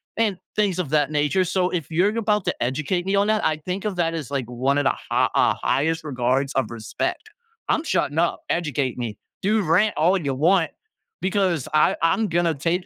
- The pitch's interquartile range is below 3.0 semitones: No, average, 5.0 semitones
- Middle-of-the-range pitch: Yes, medium, 165 Hz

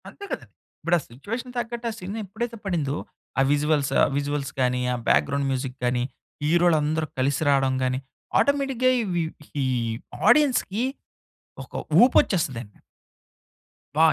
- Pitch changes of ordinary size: No, wide, 8.9 semitones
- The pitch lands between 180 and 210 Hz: No, medium, 155 Hz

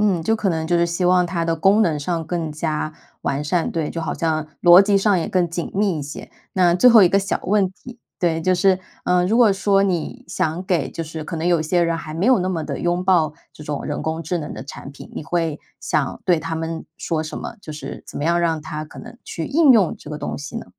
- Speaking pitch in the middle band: Yes, medium, 170 Hz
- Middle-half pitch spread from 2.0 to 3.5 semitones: Yes, average, 2.8 semitones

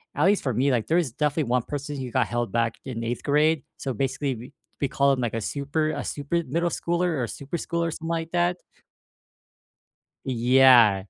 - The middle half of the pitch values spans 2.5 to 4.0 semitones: No, average, 4.6 semitones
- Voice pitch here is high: No, medium, 140 Hz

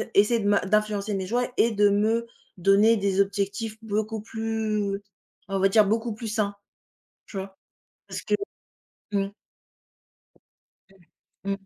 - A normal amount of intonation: No, narrow, 1.9 semitones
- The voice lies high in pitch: Yes, high, 210 Hz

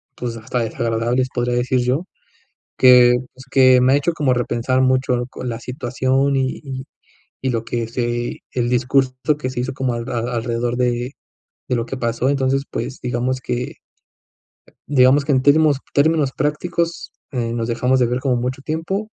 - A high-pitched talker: No, low, 130 Hz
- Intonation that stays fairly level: Yes, narrow, 1.9 semitones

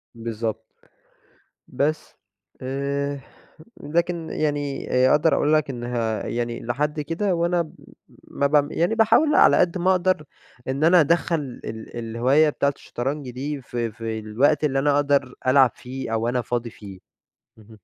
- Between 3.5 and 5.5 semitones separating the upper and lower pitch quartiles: Yes, average, 4.4 semitones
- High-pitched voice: No, medium, 140 Hz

